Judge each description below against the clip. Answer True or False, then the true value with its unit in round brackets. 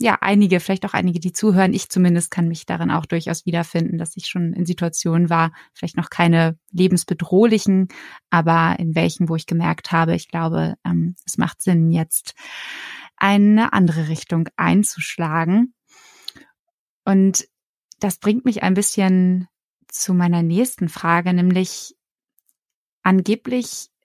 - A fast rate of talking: False (135 wpm)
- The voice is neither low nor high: True (180 Hz)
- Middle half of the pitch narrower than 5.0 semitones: True (2.9 semitones)